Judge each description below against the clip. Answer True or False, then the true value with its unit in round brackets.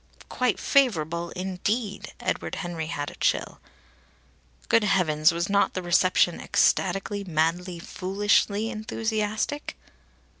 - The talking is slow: True (105 wpm)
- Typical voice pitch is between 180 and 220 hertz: True (190 Hz)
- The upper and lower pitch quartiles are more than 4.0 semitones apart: False (3.6 semitones)